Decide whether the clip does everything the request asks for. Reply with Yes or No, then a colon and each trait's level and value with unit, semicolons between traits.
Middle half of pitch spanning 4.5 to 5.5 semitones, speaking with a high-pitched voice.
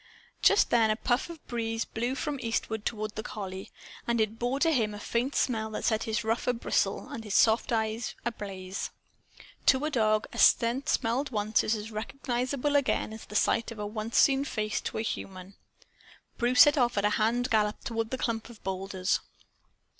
No: narrow, 2.4 semitones; high, 225 Hz